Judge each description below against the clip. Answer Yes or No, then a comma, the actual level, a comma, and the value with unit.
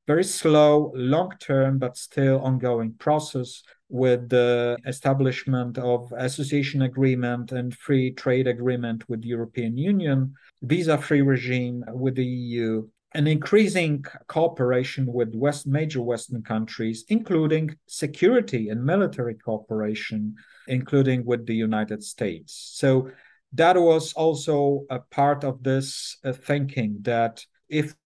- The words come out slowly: Yes, slow, 120 wpm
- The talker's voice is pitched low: Yes, low, 130 Hz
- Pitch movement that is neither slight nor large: Yes, average, 3.3 semitones